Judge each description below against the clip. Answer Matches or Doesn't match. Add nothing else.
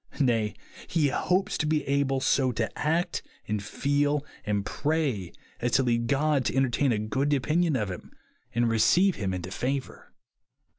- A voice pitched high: Doesn't match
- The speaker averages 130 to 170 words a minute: Matches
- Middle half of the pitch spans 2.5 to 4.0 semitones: Doesn't match